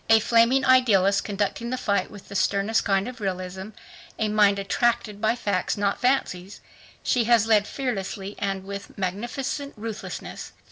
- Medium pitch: No, high, 210 Hz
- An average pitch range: Yes, average, 3.1 semitones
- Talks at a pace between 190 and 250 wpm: No, average, 150 wpm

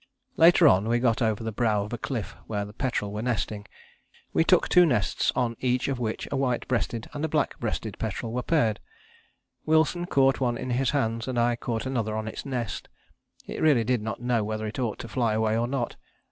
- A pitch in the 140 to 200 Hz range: No, low, 120 Hz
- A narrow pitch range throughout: No, average, 3.2 semitones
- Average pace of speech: No, fast, 215 wpm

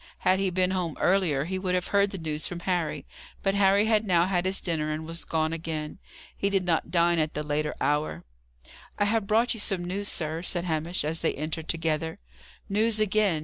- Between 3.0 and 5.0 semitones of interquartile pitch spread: Yes, average, 3.5 semitones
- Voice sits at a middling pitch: Yes, medium, 175 Hz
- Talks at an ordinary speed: No, fast, 210 wpm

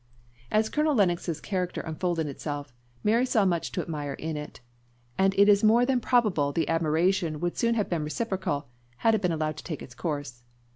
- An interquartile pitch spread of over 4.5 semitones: Yes, wide, 5.5 semitones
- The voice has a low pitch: No, medium, 175 Hz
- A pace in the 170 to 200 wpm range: Yes, average, 190 wpm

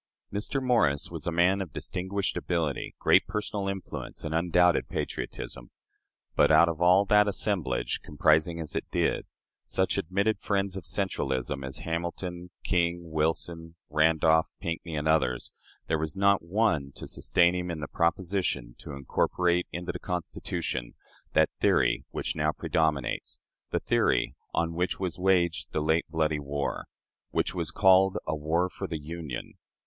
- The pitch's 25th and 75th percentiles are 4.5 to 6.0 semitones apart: No, average, 3.1 semitones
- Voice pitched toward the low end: Yes, very low, 85 Hz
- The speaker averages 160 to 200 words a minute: No, average, 150 wpm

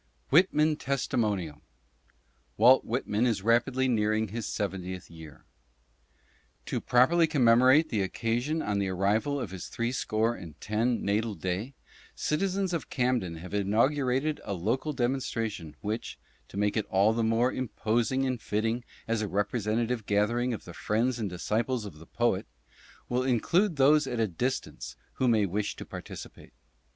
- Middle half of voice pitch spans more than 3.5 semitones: Yes, average, 4.0 semitones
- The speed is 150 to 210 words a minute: Yes, average, 155 wpm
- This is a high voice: No, low, 115 Hz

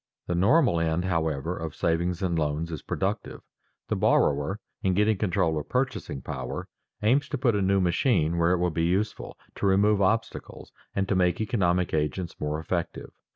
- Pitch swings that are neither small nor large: Yes, average, 3.7 semitones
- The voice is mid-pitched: No, very low, 90 Hz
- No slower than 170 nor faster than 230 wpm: Yes, average, 175 wpm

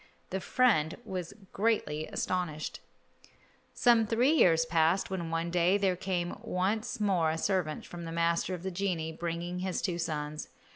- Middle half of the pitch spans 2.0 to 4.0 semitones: Yes, average, 2.8 semitones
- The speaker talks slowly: No, average, 155 wpm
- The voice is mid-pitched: Yes, medium, 175 Hz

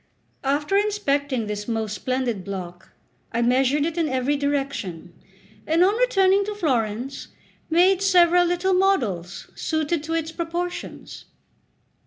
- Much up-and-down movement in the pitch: Yes, wide, 6.9 semitones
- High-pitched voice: Yes, very high, 290 Hz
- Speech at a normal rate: No, slow, 125 wpm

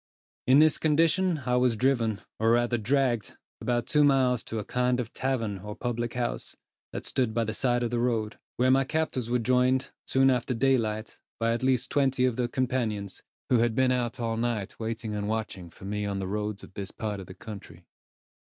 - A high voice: No, low, 120 Hz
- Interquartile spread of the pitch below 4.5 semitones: Yes, average, 2.9 semitones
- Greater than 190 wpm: Yes, fast, 205 wpm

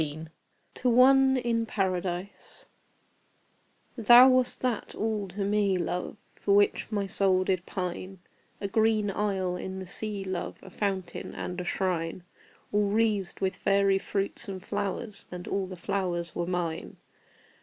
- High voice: Yes, high, 195 Hz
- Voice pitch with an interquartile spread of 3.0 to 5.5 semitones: No, narrow, 2.4 semitones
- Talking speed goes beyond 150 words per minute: No, average, 145 wpm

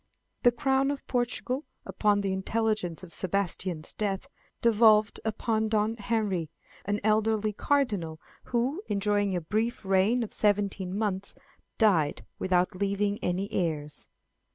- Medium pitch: No, high, 205 Hz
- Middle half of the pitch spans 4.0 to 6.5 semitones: No, average, 2.8 semitones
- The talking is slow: Yes, slow, 125 wpm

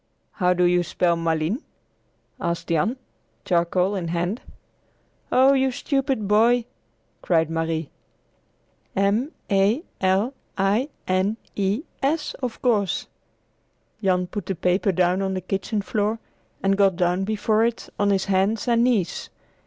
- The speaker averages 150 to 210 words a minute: No, slow, 135 wpm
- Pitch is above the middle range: Yes, high, 195 Hz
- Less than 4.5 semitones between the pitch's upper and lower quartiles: Yes, average, 3.9 semitones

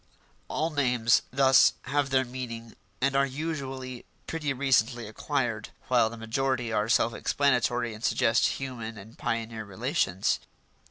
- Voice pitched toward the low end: Yes, low, 125 Hz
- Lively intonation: No, average, 3.1 semitones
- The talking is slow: Yes, slow, 130 wpm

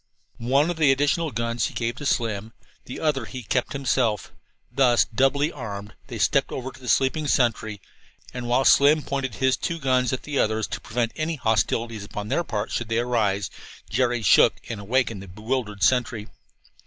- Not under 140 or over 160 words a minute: No, average, 180 wpm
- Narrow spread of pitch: No, average, 3.4 semitones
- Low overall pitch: Yes, low, 120 Hz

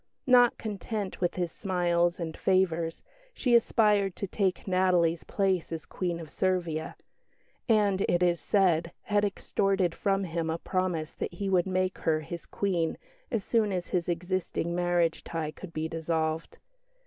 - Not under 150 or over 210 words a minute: Yes, average, 155 wpm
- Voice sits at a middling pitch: Yes, medium, 180 Hz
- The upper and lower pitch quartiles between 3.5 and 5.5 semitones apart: No, average, 2.7 semitones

